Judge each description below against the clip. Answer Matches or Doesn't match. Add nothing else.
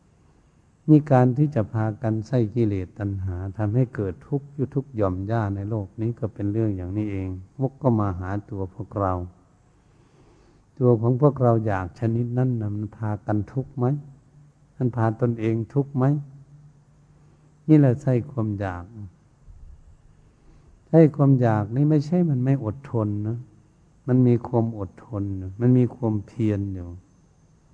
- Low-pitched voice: Matches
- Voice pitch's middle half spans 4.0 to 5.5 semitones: Matches